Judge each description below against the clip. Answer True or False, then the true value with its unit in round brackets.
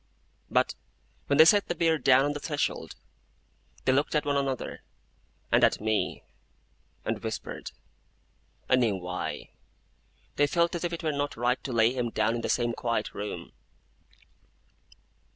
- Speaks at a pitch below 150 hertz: True (135 Hz)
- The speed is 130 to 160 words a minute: True (155 wpm)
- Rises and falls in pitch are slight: False (4.3 semitones)